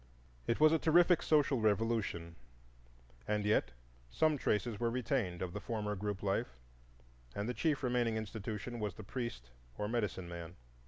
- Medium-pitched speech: No, low, 110 Hz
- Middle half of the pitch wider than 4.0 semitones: No, average, 3.7 semitones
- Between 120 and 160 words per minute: Yes, average, 155 wpm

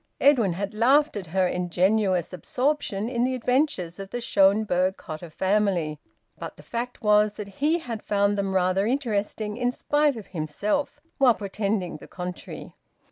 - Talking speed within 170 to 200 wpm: No, average, 155 wpm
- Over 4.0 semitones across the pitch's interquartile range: Yes, average, 4.5 semitones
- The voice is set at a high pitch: Yes, high, 205 Hz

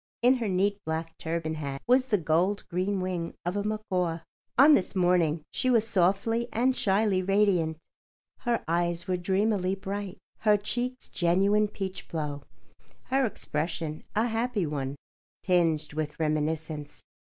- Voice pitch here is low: No, medium, 185 Hz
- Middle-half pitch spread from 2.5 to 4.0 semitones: No, average, 4.5 semitones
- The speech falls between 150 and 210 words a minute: No, average, 140 wpm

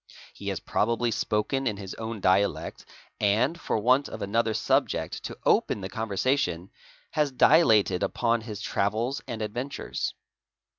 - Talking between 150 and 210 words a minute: No, average, 140 wpm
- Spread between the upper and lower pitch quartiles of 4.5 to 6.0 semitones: No, average, 3.7 semitones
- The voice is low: Yes, low, 110 Hz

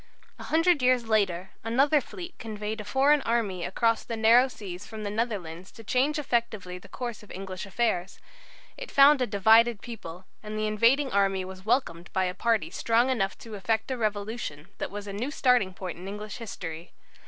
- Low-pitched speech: No, high, 215 Hz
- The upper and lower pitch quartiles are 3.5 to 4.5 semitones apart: Yes, average, 4.0 semitones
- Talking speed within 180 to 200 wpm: Yes, average, 190 wpm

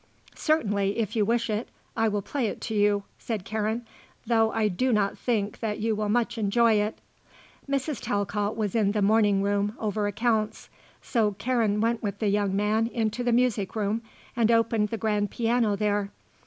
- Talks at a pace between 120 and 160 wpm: No, average, 180 wpm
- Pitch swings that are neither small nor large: No, narrow, 1.9 semitones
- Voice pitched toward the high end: Yes, high, 215 Hz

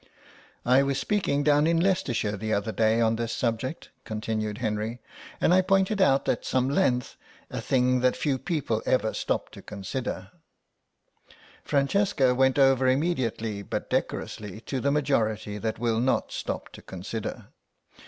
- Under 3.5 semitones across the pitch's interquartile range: No, average, 4.2 semitones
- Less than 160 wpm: Yes, average, 150 wpm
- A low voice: Yes, low, 125 Hz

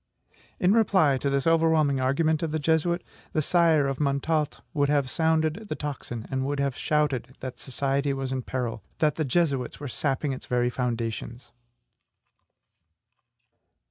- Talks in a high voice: No, medium, 140 Hz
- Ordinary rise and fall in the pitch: Yes, average, 3.3 semitones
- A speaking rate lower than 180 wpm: Yes, average, 150 wpm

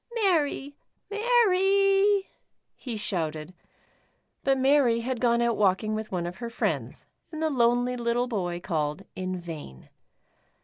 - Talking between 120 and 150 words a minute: Yes, slow, 135 wpm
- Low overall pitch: No, high, 235 Hz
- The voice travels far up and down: Yes, wide, 8.5 semitones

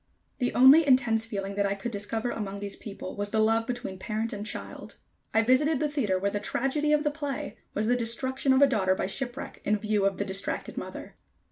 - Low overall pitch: No, high, 225 Hz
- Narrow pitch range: No, average, 4.5 semitones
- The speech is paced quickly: Yes, fast, 220 wpm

